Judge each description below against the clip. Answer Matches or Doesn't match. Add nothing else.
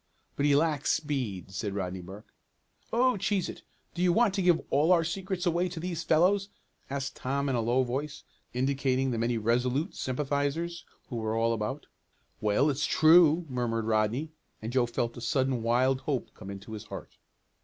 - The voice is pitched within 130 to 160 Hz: Matches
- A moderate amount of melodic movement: Doesn't match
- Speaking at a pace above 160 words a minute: Matches